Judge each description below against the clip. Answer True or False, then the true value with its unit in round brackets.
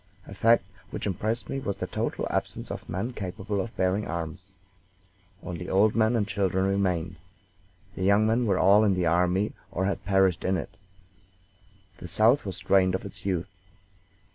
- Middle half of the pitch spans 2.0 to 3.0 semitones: True (2.5 semitones)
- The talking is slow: False (170 wpm)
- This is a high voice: False (95 Hz)